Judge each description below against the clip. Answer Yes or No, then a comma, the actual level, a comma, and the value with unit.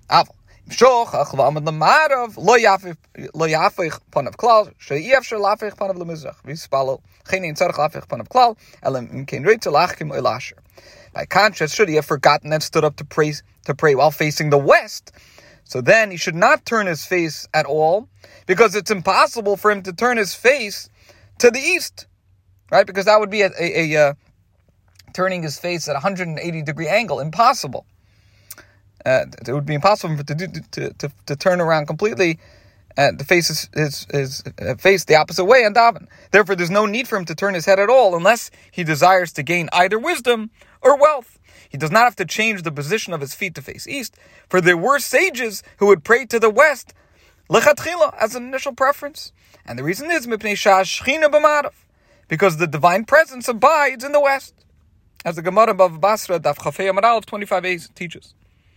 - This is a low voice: No, medium, 185 Hz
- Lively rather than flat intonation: Yes, wide, 6.7 semitones